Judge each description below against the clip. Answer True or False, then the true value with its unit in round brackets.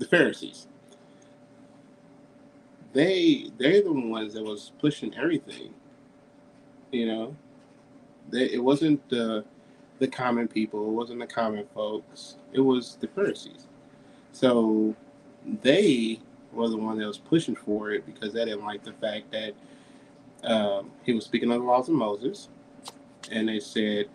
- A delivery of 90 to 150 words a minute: True (140 wpm)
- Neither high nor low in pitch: False (115 Hz)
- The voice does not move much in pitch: False (3.6 semitones)